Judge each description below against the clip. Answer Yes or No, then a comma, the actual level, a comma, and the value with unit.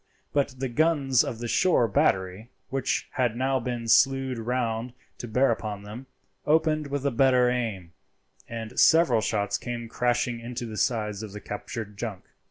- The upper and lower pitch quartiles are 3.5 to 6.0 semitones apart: No, average, 3.1 semitones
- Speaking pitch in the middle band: No, low, 120 Hz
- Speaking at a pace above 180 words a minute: No, average, 165 wpm